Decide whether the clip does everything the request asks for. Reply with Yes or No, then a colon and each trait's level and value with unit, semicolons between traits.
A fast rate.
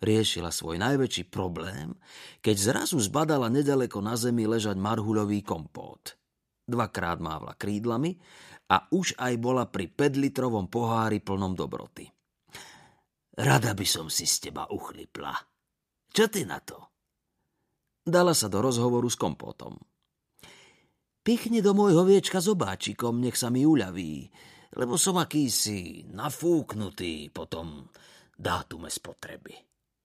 No: average, 120 wpm